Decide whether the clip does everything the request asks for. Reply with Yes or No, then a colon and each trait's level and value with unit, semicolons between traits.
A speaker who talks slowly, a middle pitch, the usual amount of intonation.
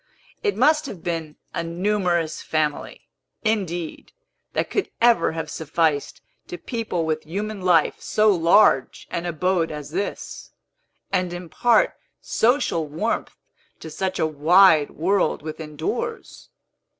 Yes: slow, 125 wpm; medium, 175 Hz; average, 4.4 semitones